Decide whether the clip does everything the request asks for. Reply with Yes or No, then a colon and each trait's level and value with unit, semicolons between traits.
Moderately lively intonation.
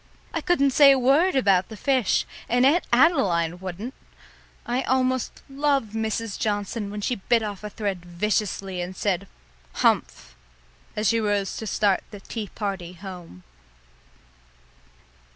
Yes: average, 4.9 semitones